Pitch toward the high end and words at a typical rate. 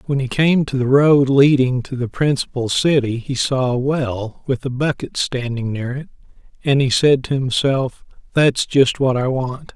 No: low, 130 Hz; average, 190 wpm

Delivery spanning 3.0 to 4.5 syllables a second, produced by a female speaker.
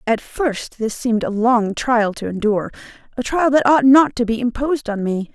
No: 5.1 syllables/s; female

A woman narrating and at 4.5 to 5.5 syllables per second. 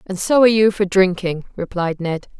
Yes: female; 5.3 syllables/s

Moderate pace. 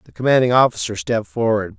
Yes: average, 170 wpm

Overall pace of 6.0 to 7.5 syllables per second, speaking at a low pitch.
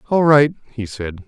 No: 4.7 syllables/s; low, 125 Hz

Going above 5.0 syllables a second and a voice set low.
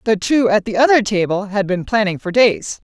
No: 5.2 syllables/s; high, 210 Hz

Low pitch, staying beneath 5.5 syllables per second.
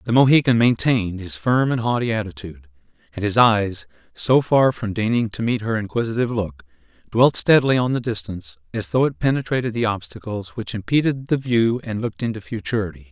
No: low, 110 Hz; 5.9 syllables/s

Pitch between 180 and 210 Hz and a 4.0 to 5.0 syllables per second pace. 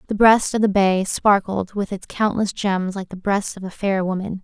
Yes: high, 195 Hz; 4.7 syllables/s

